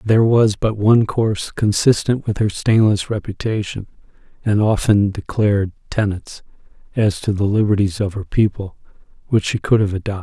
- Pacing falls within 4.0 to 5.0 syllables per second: No, 5.2 syllables/s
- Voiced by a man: Yes, male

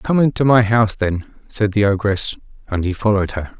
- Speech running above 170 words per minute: Yes, average, 200 wpm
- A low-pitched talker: Yes, low, 105 Hz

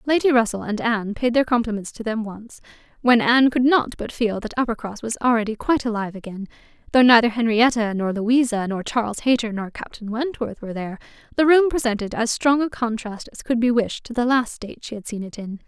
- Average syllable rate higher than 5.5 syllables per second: Yes, 5.9 syllables/s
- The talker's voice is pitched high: Yes, high, 230 Hz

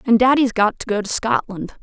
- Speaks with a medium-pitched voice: No, high, 220 Hz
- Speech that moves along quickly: Yes, fast, 230 wpm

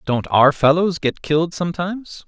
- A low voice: No, medium, 160 Hz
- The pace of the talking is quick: No, average, 160 wpm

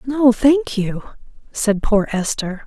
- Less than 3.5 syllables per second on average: Yes, 3.2 syllables/s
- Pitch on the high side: Yes, high, 230 Hz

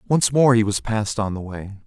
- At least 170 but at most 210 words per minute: No, fast, 255 wpm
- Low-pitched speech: Yes, low, 110 Hz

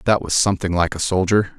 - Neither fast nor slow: No, fast, 230 wpm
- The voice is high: No, very low, 95 Hz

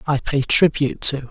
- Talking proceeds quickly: No, average, 185 wpm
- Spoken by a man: Yes, male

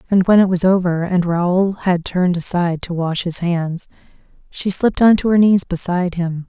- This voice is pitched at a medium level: Yes, medium, 180 Hz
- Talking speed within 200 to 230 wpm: Yes, fast, 205 wpm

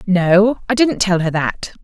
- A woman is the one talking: Yes, female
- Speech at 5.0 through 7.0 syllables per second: No, 3.8 syllables/s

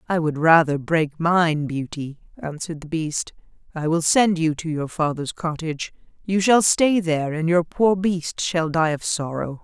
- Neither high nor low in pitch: Yes, medium, 165 Hz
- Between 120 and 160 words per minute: No, average, 180 wpm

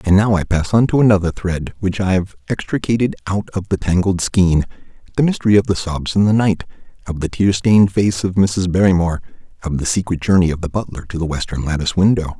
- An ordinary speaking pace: No, fast, 220 wpm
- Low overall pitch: Yes, very low, 95 Hz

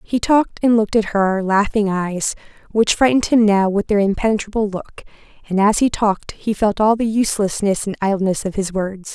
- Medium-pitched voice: No, high, 205 Hz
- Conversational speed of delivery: Yes, average, 195 wpm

